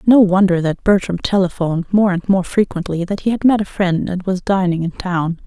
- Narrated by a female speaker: Yes, female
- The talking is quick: Yes, fast, 220 wpm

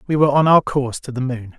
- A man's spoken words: Yes, male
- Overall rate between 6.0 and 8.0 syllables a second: Yes, 7.0 syllables/s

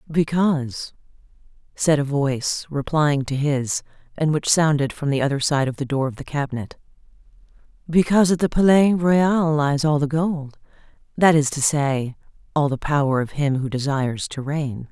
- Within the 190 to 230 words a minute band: No, average, 165 wpm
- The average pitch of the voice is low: No, medium, 145 Hz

